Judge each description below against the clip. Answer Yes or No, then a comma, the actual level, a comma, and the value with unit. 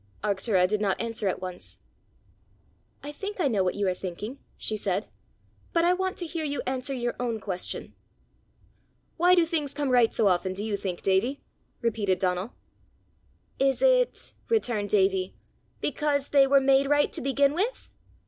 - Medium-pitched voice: No, high, 245 Hz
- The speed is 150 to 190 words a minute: Yes, average, 165 wpm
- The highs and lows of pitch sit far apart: Yes, wide, 6.7 semitones